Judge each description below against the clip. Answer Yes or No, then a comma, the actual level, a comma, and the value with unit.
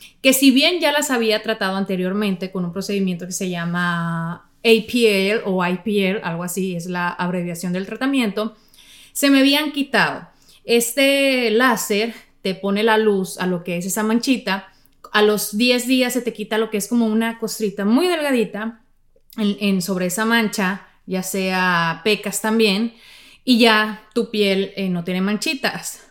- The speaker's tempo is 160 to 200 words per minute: Yes, average, 165 wpm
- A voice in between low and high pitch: No, high, 210 Hz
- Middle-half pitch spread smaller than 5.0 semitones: Yes, average, 3.5 semitones